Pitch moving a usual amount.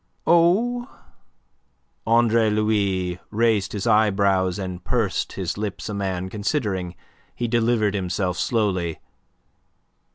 Yes: average, 3.5 semitones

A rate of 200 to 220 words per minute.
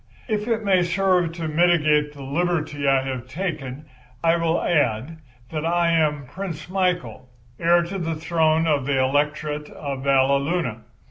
No: average, 150 wpm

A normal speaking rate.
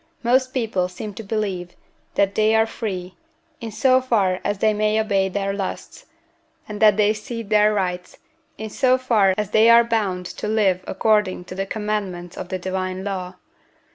Yes: average, 175 wpm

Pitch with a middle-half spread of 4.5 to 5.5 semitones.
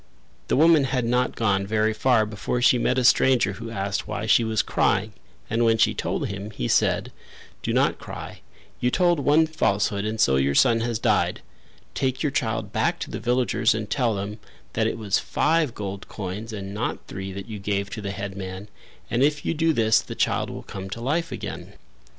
No: average, 3.9 semitones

